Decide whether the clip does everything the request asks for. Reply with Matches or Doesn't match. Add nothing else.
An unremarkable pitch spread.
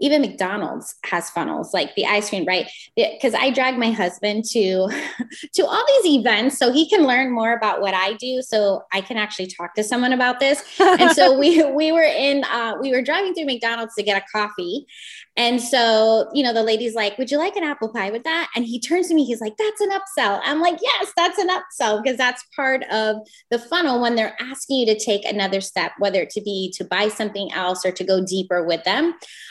Doesn't match